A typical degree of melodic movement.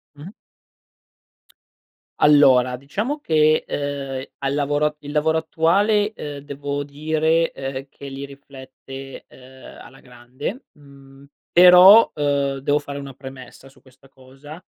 No: narrow, 2.3 semitones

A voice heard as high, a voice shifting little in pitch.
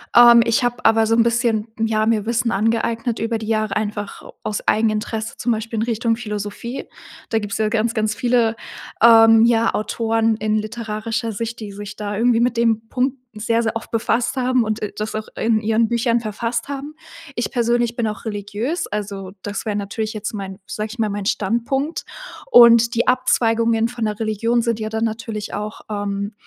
Yes: high, 225 Hz; narrow, 1.7 semitones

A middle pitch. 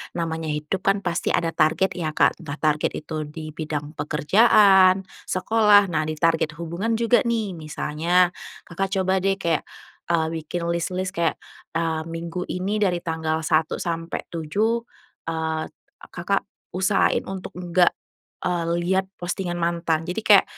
Yes: medium, 170 Hz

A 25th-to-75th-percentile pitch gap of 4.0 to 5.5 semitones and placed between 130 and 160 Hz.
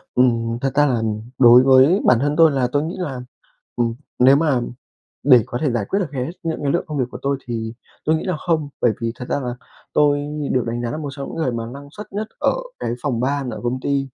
No: average, 3.4 semitones; low, 135 Hz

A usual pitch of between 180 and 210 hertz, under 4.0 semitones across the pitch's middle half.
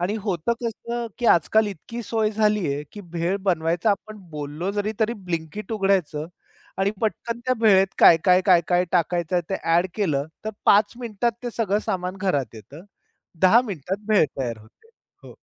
No: high, 190 Hz; average, 4.4 semitones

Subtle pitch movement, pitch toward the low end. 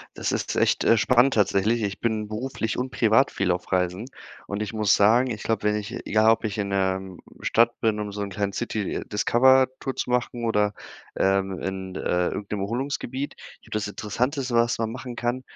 No: average, 3.2 semitones; low, 110 Hz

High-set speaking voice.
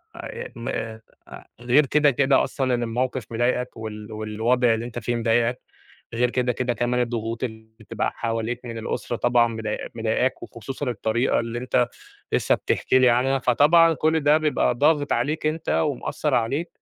No: low, 120 Hz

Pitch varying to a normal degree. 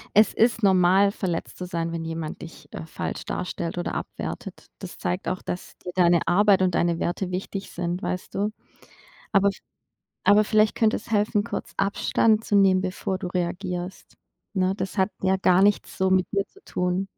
No: narrow, 2.3 semitones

